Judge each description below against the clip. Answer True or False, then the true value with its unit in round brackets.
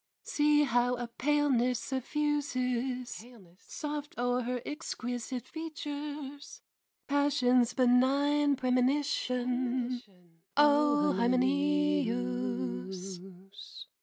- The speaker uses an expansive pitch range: False (3.2 semitones)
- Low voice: False (255 Hz)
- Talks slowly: True (65 wpm)